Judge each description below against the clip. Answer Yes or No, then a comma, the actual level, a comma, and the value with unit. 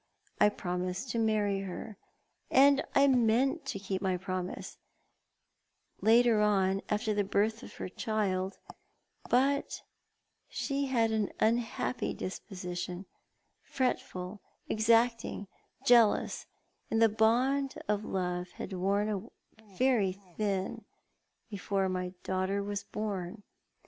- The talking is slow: Yes, slow, 110 wpm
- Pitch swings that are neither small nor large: Yes, average, 3.4 semitones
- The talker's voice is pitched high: Yes, high, 210 Hz